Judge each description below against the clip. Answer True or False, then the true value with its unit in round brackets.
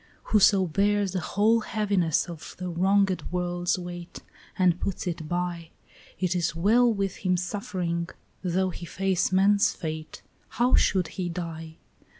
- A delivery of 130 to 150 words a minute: True (145 wpm)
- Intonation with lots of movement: False (2.4 semitones)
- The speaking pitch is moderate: True (180 Hz)